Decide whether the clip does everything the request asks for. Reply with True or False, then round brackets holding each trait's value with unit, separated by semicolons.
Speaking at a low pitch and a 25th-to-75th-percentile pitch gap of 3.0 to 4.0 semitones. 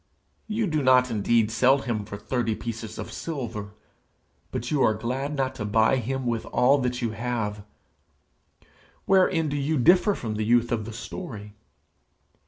True (120 Hz; 3.7 semitones)